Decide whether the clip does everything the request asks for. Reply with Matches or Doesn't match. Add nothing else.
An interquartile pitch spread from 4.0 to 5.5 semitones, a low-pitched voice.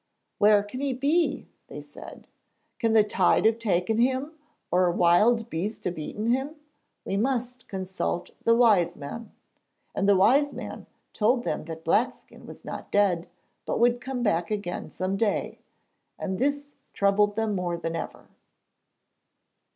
Doesn't match